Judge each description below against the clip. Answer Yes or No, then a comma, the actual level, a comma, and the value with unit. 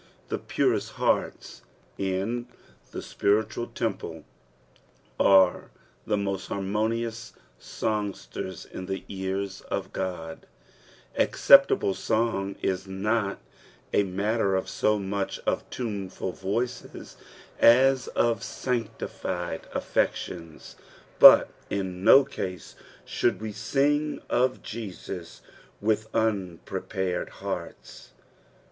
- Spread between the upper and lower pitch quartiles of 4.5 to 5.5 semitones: No, average, 3.1 semitones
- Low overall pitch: Yes, low, 100 Hz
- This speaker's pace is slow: Yes, slow, 90 wpm